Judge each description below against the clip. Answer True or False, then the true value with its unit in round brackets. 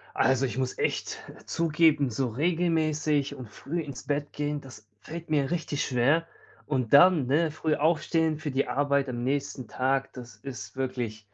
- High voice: False (140 Hz)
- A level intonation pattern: False (3.2 semitones)